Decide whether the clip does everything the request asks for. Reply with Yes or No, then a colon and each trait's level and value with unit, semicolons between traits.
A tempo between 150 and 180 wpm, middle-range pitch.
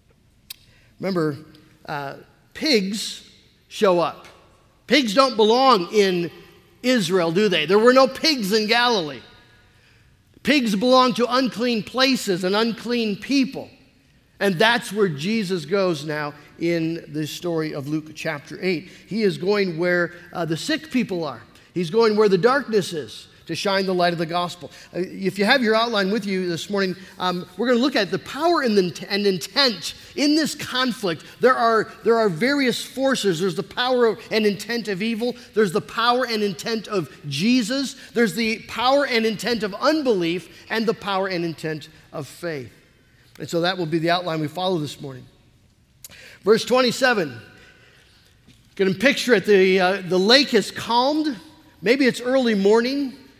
No: average, 165 wpm; high, 200 Hz